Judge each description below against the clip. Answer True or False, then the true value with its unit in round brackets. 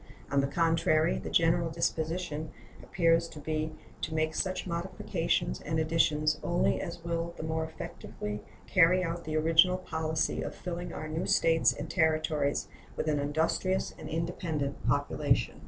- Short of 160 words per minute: True (150 wpm)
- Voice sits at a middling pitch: True (160 Hz)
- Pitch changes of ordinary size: False (1.5 semitones)